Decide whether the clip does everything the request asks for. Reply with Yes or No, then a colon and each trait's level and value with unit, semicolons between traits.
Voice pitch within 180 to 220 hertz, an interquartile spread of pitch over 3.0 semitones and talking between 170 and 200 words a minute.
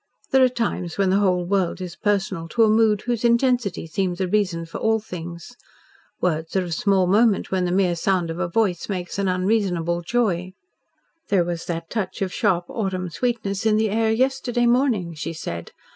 Yes: high, 190 Hz; average, 4.1 semitones; average, 190 wpm